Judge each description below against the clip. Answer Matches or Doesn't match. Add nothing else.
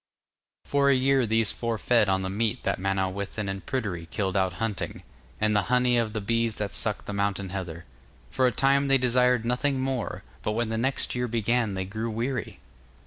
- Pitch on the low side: Matches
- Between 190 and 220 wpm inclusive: Matches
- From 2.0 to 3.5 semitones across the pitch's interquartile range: Doesn't match